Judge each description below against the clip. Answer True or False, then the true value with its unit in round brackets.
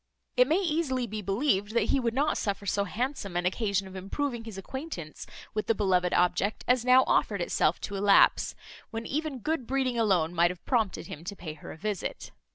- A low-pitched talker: False (215 Hz)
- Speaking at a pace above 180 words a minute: True (200 wpm)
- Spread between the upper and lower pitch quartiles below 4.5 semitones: False (5.2 semitones)